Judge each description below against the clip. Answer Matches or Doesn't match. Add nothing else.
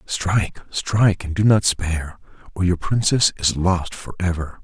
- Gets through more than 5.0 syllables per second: Doesn't match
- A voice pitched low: Matches